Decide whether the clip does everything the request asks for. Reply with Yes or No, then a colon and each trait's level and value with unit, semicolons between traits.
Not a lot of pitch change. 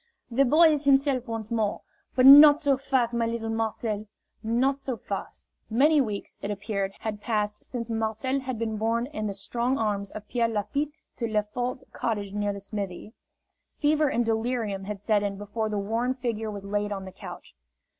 No: average, 3.5 semitones